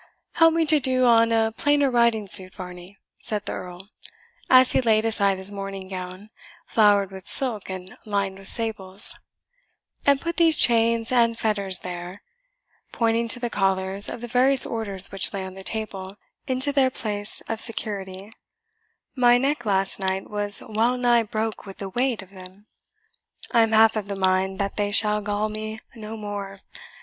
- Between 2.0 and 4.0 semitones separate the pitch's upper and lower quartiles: Yes, average, 3.2 semitones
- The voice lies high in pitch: Yes, high, 210 Hz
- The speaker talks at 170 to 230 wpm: Yes, average, 175 wpm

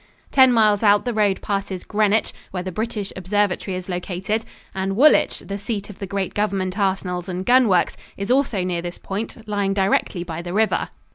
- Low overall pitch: No, high, 200 Hz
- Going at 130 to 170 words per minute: No, average, 190 wpm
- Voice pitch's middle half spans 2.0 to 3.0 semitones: Yes, narrow, 2.5 semitones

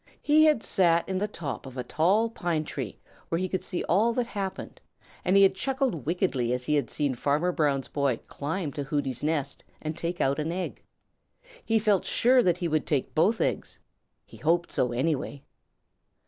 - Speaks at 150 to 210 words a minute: Yes, average, 190 wpm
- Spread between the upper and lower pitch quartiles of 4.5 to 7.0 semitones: Yes, wide, 5.4 semitones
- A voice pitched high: No, medium, 165 Hz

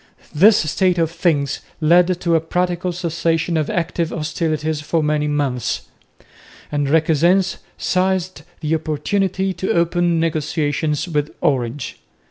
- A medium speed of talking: No, slow, 120 wpm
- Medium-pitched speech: Yes, medium, 165 Hz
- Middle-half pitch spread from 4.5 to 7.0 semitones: No, average, 2.8 semitones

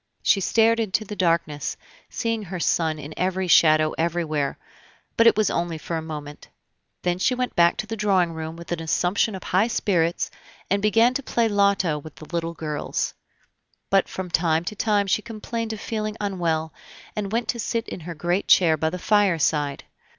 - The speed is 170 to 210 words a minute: Yes, average, 190 wpm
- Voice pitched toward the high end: No, medium, 180 Hz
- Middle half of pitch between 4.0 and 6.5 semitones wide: Yes, average, 4.6 semitones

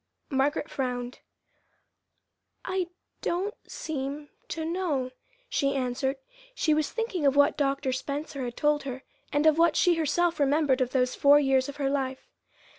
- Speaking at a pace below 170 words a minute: Yes, average, 150 wpm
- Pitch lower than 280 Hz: No, very high, 285 Hz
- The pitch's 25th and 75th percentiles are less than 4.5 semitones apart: Yes, average, 2.9 semitones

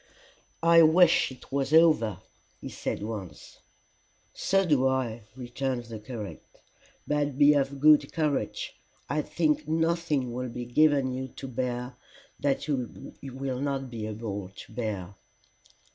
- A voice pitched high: No, low, 130 Hz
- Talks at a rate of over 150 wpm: No, slow, 135 wpm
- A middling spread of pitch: Yes, average, 3.8 semitones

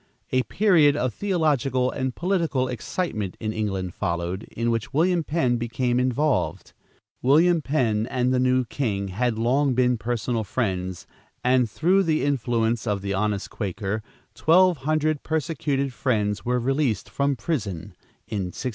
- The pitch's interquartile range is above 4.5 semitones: Yes, average, 5.1 semitones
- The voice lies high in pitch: No, low, 125 Hz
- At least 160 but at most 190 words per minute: No, average, 145 wpm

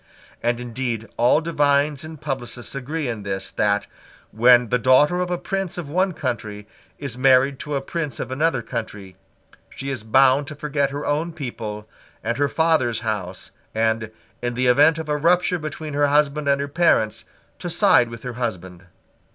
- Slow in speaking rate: No, average, 175 wpm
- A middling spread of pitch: Yes, average, 4.4 semitones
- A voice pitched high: No, low, 135 Hz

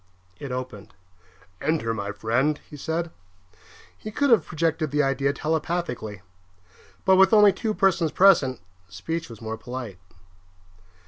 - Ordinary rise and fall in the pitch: No, wide, 6.9 semitones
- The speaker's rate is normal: No, slow, 130 wpm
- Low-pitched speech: No, medium, 150 Hz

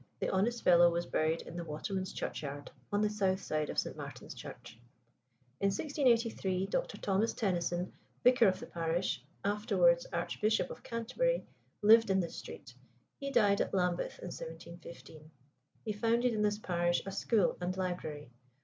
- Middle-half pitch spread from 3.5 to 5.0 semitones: Yes, average, 4.7 semitones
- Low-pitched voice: No, high, 190 Hz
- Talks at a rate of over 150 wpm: Yes, average, 160 wpm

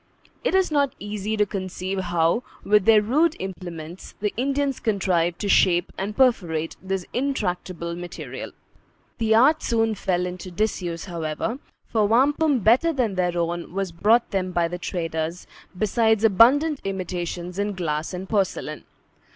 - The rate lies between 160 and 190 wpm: No, average, 145 wpm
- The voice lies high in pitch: Yes, high, 195 Hz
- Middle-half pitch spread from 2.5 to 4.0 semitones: No, average, 4.4 semitones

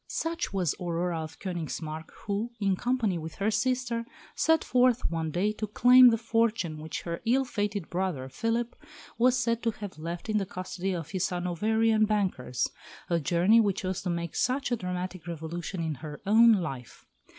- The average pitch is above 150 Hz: Yes, high, 190 Hz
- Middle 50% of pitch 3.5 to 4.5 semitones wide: No, average, 5.1 semitones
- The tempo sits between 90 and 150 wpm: No, average, 175 wpm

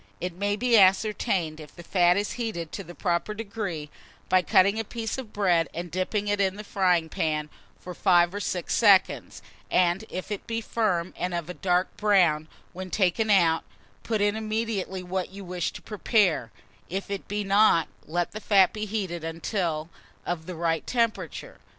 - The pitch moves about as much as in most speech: Yes, average, 3.3 semitones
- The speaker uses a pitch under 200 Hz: Yes, medium, 185 Hz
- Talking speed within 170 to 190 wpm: Yes, average, 180 wpm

